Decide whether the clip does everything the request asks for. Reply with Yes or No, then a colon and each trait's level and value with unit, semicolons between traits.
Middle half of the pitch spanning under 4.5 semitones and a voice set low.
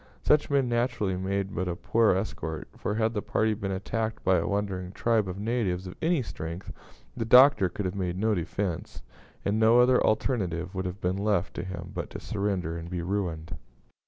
Yes: average, 3.5 semitones; low, 100 Hz